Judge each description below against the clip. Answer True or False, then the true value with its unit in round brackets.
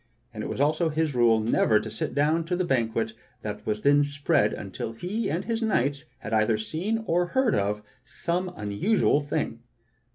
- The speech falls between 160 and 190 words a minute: True (185 wpm)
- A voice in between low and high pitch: True (145 Hz)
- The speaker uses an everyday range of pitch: False (7.8 semitones)